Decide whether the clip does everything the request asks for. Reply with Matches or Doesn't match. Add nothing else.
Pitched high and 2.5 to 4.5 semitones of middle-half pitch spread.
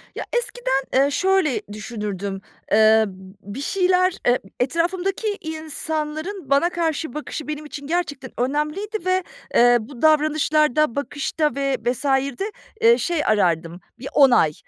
Doesn't match